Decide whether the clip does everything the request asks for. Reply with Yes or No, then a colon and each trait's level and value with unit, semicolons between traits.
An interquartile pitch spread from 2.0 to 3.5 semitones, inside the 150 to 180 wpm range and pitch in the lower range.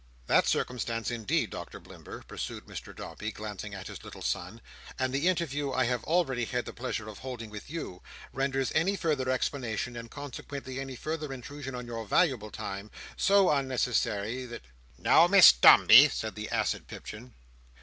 No: average, 3.9 semitones; average, 165 wpm; low, 125 Hz